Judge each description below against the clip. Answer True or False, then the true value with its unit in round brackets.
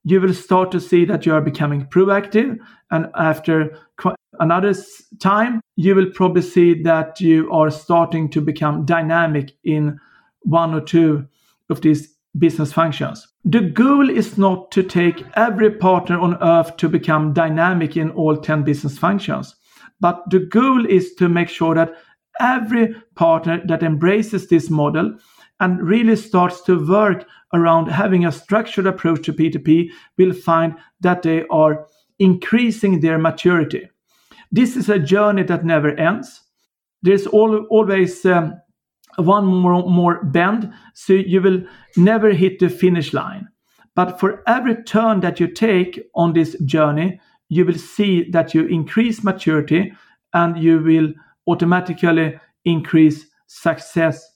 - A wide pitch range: False (3.2 semitones)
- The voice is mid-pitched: True (175 Hz)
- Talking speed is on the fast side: False (145 wpm)